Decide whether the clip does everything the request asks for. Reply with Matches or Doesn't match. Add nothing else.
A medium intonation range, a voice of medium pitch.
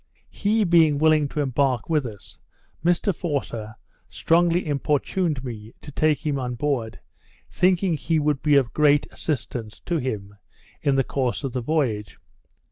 Matches